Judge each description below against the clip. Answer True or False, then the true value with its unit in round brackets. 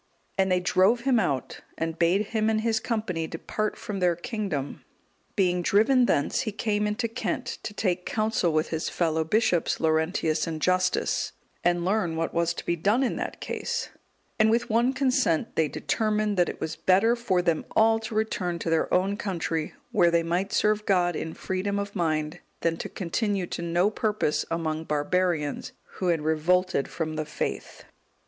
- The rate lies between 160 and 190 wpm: True (180 wpm)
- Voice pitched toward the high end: False (180 Hz)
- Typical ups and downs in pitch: True (4.6 semitones)